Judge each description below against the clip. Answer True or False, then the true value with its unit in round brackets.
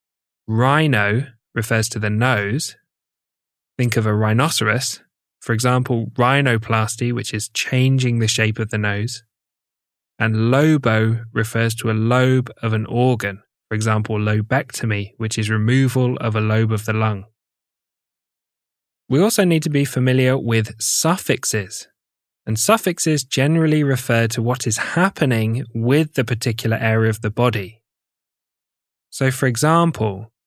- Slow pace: True (130 wpm)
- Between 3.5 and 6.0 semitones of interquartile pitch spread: False (3.0 semitones)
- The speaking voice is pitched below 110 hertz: False (115 Hz)